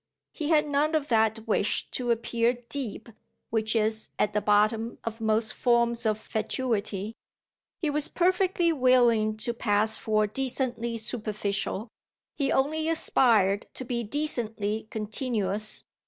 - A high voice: Yes, high, 230 Hz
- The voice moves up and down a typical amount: Yes, average, 3.3 semitones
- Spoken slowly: Yes, slow, 130 wpm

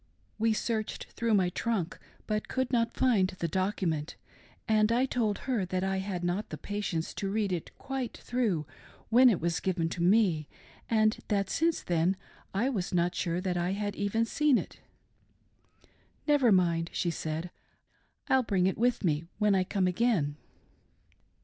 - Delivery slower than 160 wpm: No, average, 170 wpm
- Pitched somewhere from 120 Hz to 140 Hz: No, high, 195 Hz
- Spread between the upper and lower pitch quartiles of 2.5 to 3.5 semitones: No, average, 4.4 semitones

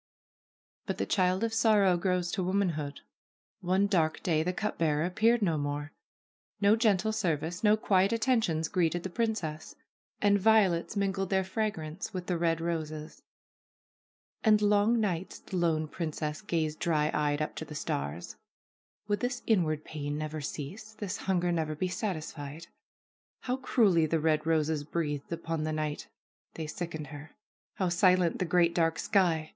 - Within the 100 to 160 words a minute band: Yes, average, 155 wpm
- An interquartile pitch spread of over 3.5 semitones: Yes, average, 4.3 semitones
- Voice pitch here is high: No, medium, 170 Hz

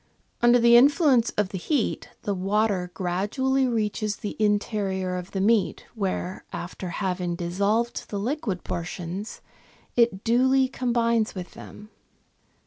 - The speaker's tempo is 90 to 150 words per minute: Yes, slow, 135 wpm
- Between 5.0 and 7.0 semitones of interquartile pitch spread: No, average, 4.1 semitones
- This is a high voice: Yes, high, 210 Hz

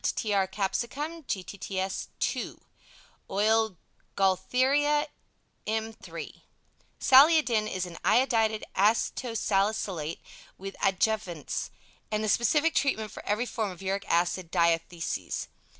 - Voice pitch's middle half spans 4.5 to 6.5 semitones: No, average, 3.8 semitones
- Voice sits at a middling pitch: No, high, 210 Hz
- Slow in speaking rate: Yes, slow, 105 wpm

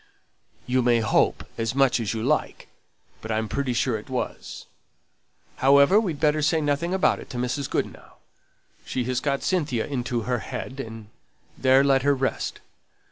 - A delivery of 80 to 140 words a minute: No, average, 165 wpm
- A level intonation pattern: No, average, 3.0 semitones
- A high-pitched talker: No, low, 130 Hz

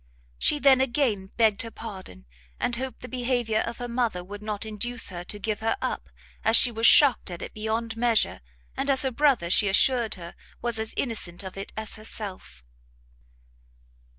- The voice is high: Yes, high, 225 Hz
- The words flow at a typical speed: Yes, average, 180 wpm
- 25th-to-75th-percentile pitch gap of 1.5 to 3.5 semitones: Yes, average, 3.1 semitones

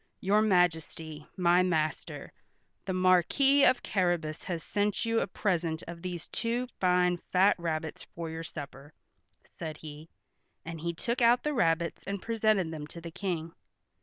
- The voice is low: No, medium, 175 Hz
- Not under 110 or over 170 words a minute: Yes, average, 155 wpm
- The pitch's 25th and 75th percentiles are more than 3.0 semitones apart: Yes, average, 3.7 semitones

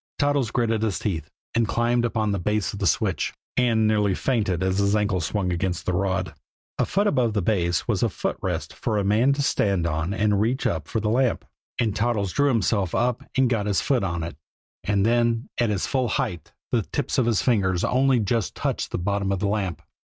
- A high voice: No, low, 105 Hz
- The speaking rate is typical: No, fast, 215 wpm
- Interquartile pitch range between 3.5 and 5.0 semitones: Yes, average, 3.8 semitones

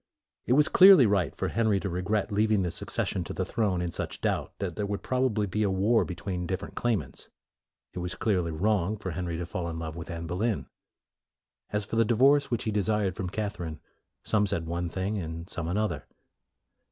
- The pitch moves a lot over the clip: No, average, 3.7 semitones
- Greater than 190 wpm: Yes, average, 200 wpm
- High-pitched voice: No, low, 100 Hz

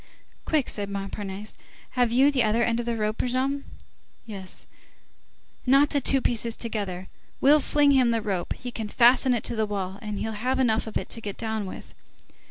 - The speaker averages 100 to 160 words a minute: No, average, 190 wpm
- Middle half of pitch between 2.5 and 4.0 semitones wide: Yes, average, 3.5 semitones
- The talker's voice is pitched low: No, high, 230 Hz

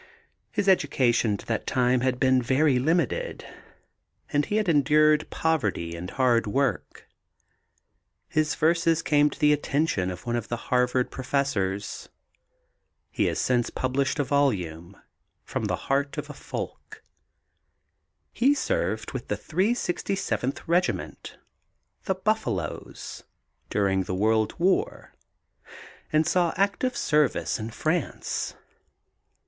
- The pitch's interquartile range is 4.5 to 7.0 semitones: Yes, wide, 5.5 semitones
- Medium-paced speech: No, slow, 120 wpm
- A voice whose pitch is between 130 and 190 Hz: Yes, medium, 140 Hz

